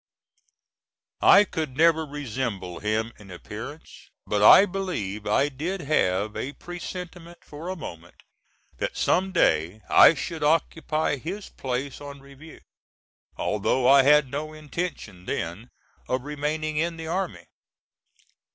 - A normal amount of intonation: No, wide, 6.8 semitones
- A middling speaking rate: No, slow, 125 wpm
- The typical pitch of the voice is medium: Yes, medium, 145 Hz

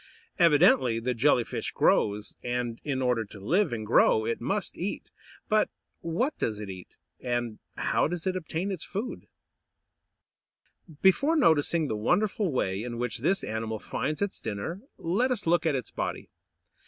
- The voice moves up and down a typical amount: No, wide, 8.3 semitones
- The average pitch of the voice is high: No, medium, 145 Hz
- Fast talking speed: No, average, 165 wpm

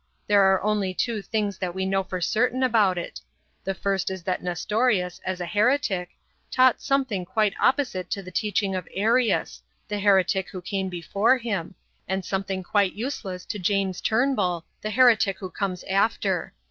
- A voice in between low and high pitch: No, high, 195 Hz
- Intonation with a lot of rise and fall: No, average, 2.8 semitones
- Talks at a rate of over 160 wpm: Yes, average, 170 wpm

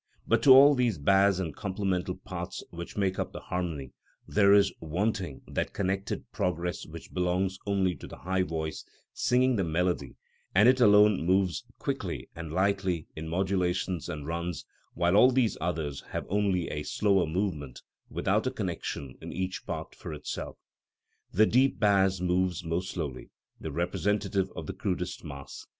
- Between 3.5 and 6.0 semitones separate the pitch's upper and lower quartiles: No, average, 2.8 semitones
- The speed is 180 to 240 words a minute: No, average, 160 wpm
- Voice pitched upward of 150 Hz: No, very low, 95 Hz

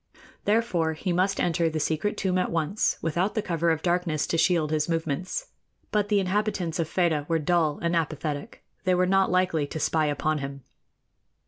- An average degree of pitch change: Yes, average, 3.0 semitones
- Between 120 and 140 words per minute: No, average, 185 wpm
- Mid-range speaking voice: Yes, medium, 170 Hz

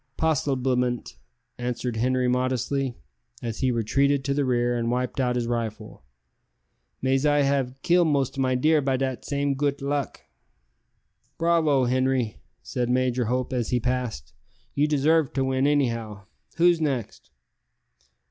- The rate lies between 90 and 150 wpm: Yes, average, 140 wpm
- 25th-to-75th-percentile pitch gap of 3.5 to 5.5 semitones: No, narrow, 2.4 semitones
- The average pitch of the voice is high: No, low, 130 Hz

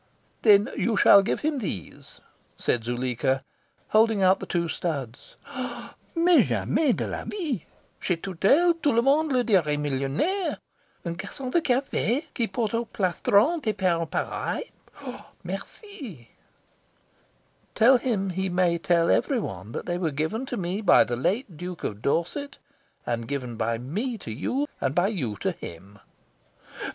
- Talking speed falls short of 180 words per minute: Yes, average, 150 wpm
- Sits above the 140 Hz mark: Yes, high, 190 Hz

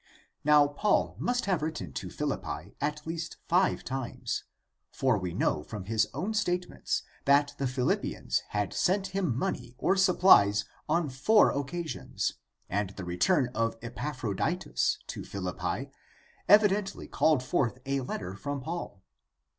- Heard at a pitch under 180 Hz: Yes, medium, 140 Hz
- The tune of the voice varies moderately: No, wide, 7.4 semitones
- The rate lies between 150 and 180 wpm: No, slow, 135 wpm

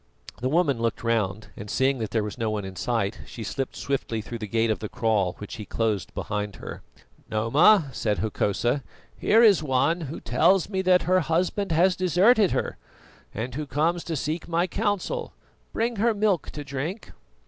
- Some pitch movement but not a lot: No, wide, 8.4 semitones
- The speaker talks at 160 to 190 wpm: Yes, average, 185 wpm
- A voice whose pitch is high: No, medium, 140 Hz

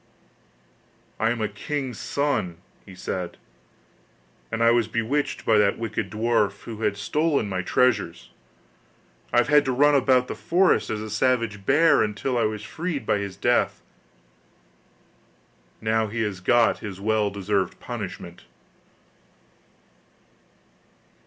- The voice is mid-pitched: No, low, 110 Hz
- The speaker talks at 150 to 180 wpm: No, slow, 135 wpm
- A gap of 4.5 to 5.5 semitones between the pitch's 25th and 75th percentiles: No, average, 3.8 semitones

